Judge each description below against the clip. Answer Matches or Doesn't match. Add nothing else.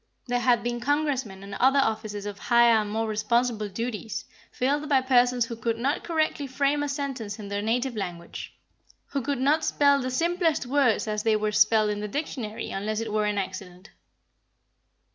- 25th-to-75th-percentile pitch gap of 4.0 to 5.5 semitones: Matches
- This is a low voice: Doesn't match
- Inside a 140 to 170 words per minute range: Doesn't match